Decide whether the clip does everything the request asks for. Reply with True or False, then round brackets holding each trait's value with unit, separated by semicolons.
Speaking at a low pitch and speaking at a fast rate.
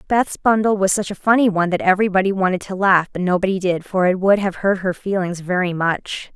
False (190 Hz; 225 wpm)